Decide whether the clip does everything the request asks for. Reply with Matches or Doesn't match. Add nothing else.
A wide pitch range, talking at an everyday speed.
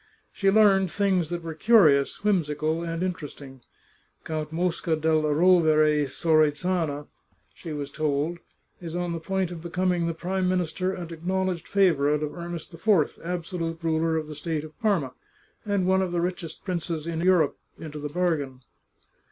Doesn't match